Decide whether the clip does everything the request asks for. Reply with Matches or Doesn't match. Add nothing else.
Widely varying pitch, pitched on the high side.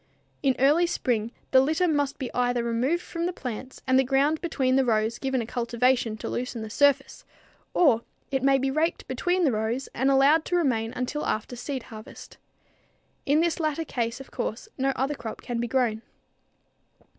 Doesn't match